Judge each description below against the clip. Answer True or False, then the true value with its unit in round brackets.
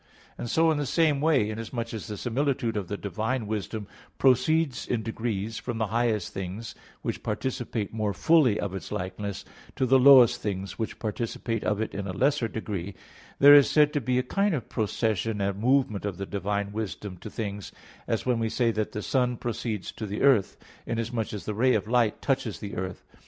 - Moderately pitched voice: False (115 Hz)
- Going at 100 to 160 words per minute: False (200 wpm)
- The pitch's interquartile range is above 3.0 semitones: True (3.7 semitones)